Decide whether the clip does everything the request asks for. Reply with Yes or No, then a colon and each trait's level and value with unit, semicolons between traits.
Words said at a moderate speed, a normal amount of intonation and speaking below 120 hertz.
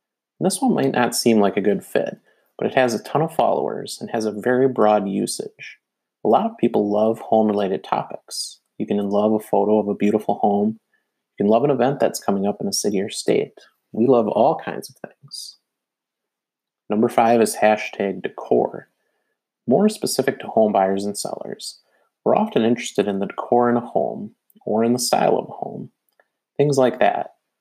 Yes: average, 195 wpm; average, 3.0 semitones; low, 110 Hz